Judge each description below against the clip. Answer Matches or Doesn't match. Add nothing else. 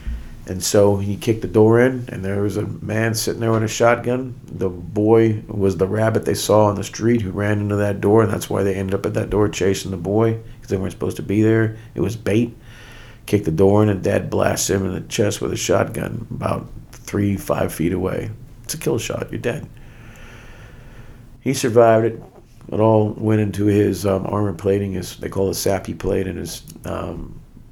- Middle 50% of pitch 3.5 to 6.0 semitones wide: Doesn't match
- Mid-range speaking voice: Doesn't match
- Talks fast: Matches